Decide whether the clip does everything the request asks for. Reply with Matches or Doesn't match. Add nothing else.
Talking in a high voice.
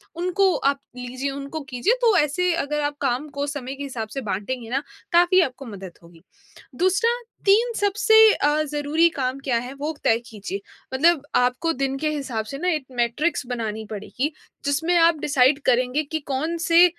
Matches